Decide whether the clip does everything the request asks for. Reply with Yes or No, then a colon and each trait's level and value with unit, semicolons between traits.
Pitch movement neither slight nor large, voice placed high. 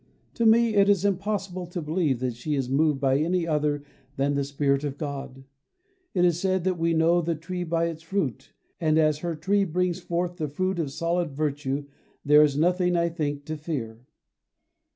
No: average, 3.7 semitones; medium, 160 Hz